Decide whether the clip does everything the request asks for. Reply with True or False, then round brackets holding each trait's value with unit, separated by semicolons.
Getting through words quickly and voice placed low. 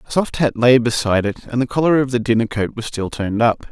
True (275 wpm; 120 Hz)